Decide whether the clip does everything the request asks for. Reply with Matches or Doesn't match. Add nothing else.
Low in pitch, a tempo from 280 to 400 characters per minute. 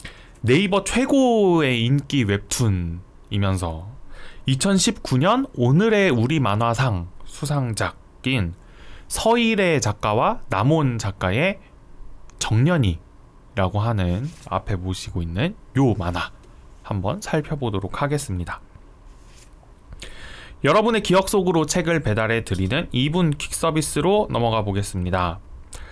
Doesn't match